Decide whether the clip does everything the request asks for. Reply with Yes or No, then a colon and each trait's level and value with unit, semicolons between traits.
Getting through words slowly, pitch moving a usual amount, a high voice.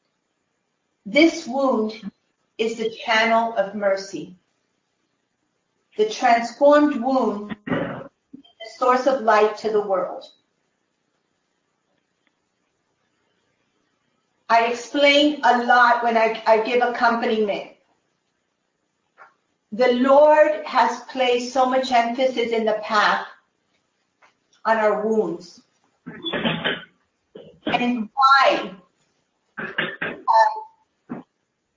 Yes: slow, 80 wpm; average, 3.2 semitones; high, 235 Hz